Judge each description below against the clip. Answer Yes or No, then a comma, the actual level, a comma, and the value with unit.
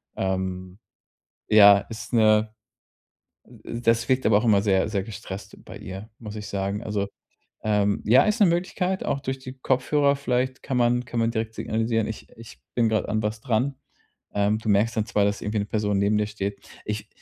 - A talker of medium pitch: No, low, 110 Hz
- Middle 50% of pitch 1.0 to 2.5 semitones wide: No, average, 2.9 semitones